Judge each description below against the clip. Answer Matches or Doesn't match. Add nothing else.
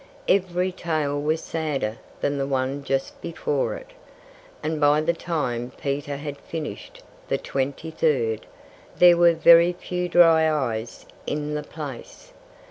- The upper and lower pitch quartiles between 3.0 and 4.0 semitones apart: Matches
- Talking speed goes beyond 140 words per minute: Doesn't match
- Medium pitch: Matches